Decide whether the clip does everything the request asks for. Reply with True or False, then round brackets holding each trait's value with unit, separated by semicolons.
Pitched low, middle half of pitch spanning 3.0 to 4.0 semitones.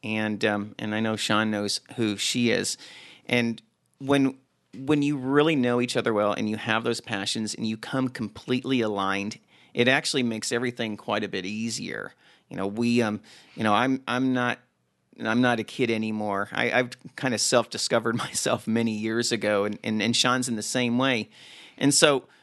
False (115 Hz; 2.6 semitones)